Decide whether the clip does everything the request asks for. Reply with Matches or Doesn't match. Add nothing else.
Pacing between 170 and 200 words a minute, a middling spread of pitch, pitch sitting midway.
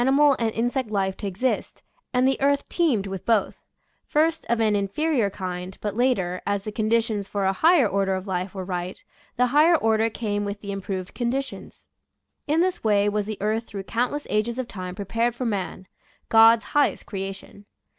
Doesn't match